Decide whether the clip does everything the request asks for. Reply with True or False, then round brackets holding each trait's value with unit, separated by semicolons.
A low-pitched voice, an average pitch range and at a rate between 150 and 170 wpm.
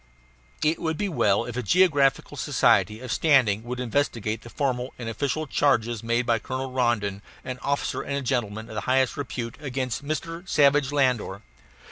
True (130 Hz; 3.5 semitones; 165 wpm)